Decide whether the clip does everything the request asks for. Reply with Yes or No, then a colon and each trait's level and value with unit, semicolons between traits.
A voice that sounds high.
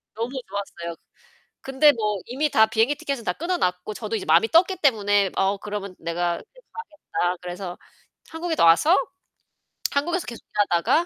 Yes: high, 220 Hz